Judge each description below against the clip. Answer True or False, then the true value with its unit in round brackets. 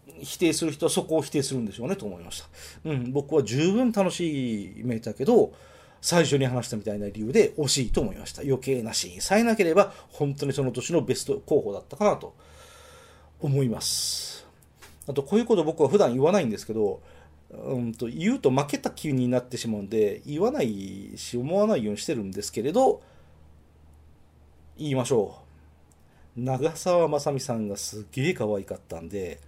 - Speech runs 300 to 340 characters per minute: False (375 characters per minute)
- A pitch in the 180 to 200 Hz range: False (130 Hz)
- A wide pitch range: True (8.2 semitones)